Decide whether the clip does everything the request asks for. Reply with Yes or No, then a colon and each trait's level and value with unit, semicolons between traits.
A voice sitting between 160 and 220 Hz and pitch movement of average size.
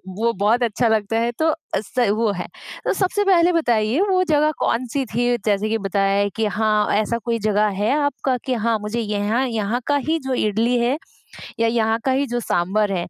No: high, 230 Hz; average, 3.2 semitones